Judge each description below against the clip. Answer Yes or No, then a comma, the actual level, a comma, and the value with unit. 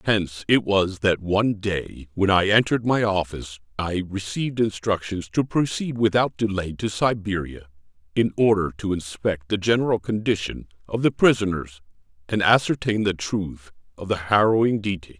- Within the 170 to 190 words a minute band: No, average, 150 wpm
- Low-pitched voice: Yes, low, 100 Hz